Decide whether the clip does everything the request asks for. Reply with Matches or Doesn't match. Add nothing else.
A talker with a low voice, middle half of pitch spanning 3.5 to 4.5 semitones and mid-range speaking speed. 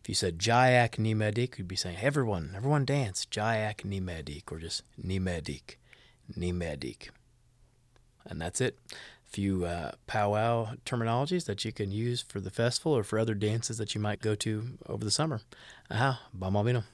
Matches